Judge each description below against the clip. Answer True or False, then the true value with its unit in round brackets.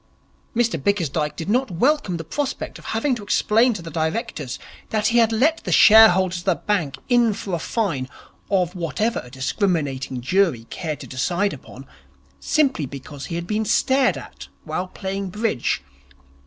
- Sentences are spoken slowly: False (170 wpm)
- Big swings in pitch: True (6.2 semitones)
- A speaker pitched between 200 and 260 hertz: False (185 Hz)